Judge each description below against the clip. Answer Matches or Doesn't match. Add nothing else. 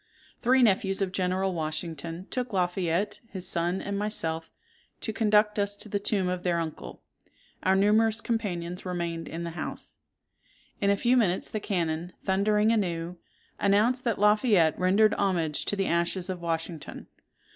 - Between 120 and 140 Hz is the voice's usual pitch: Doesn't match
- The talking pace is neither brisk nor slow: Matches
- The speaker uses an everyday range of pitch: Matches